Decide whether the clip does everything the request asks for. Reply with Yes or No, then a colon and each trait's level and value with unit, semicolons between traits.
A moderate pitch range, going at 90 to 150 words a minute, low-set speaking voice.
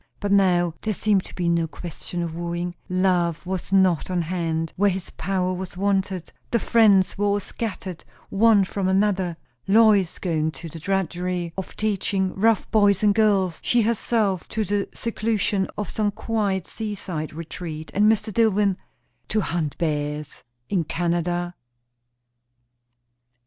No: average, 3.0 semitones; average, 145 wpm; high, 190 Hz